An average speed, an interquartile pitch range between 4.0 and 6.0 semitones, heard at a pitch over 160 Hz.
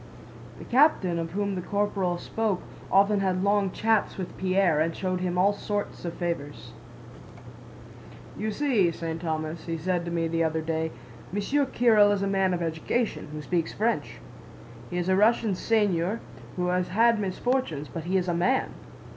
No: average, 170 wpm; average, 3.5 semitones; medium, 185 Hz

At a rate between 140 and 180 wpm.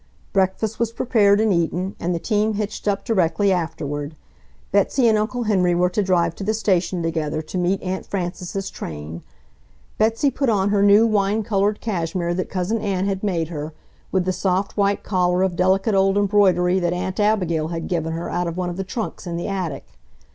No: average, 195 wpm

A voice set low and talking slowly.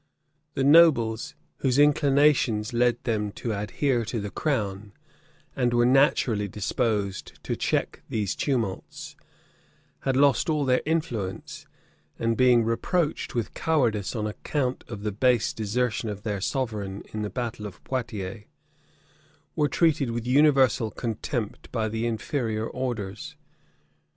Yes: low, 115 Hz; slow, 130 wpm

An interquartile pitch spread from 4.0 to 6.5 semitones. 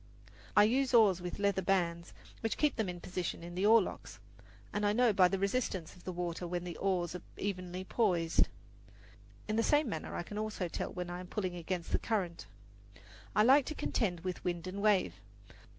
No: average, 3.2 semitones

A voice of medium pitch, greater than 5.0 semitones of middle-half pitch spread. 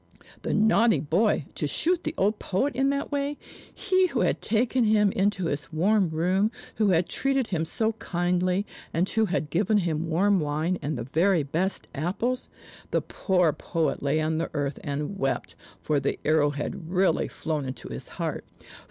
Yes: medium, 180 Hz; wide, 5.5 semitones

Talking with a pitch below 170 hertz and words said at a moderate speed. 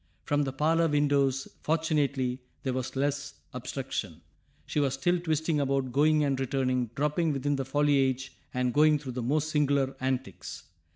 Yes: medium, 140 Hz; average, 155 wpm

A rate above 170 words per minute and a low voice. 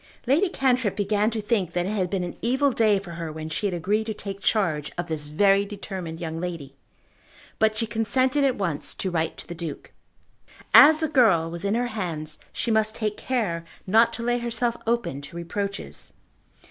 No: average, 200 wpm; high, 200 Hz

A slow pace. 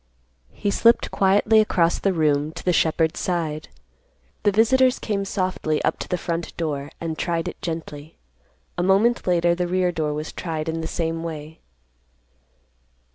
No: average, 160 wpm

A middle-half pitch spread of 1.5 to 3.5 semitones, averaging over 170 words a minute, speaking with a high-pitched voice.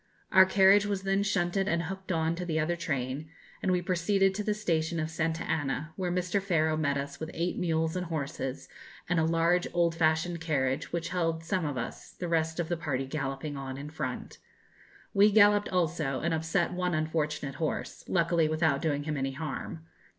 No: narrow, 2.6 semitones; average, 195 wpm; medium, 165 Hz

